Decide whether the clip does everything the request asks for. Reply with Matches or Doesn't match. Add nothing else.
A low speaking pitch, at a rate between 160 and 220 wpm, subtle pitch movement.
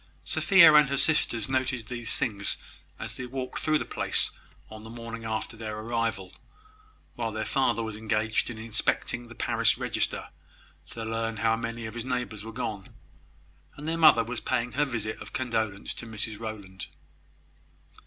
Matches